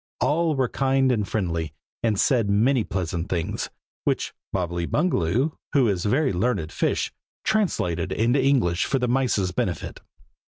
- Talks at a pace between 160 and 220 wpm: No, average, 150 wpm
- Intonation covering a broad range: Yes, wide, 6.9 semitones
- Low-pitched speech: Yes, low, 110 Hz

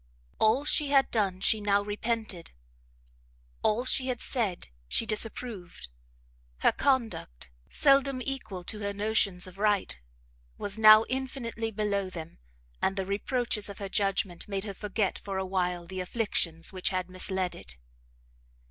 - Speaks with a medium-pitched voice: No, high, 205 Hz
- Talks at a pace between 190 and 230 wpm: No, average, 145 wpm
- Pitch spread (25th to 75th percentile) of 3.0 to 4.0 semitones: Yes, average, 3.4 semitones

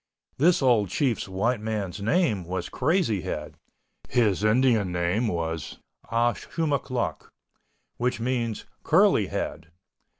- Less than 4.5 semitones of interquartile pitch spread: No, average, 5.2 semitones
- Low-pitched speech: Yes, low, 110 Hz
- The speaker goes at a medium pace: No, slow, 110 wpm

